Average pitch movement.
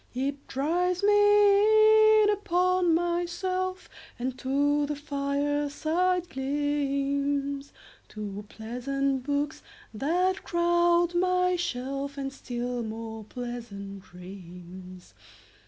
No: wide, 6.1 semitones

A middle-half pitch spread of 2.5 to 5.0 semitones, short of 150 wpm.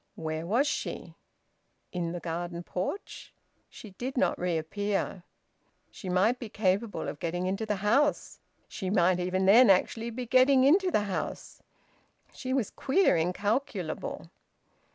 No: wide, 5.6 semitones; slow, 135 wpm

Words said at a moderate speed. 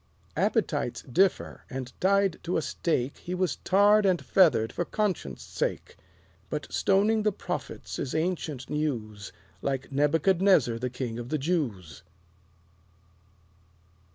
No: slow, 125 wpm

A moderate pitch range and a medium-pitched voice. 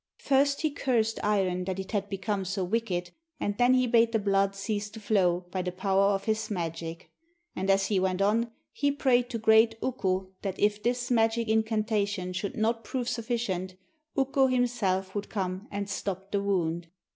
No: average, 3.4 semitones; high, 205 Hz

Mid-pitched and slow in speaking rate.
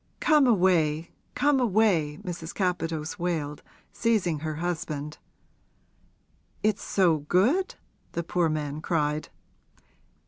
Yes: medium, 170 Hz; slow, 100 wpm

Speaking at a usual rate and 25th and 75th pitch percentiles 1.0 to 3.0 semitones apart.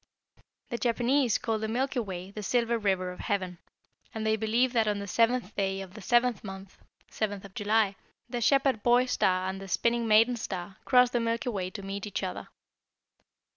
No: average, 190 wpm; average, 3.6 semitones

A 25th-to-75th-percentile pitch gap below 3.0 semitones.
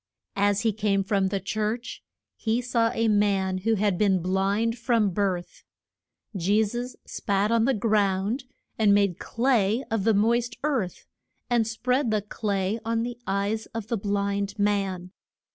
Yes: narrow, 2.5 semitones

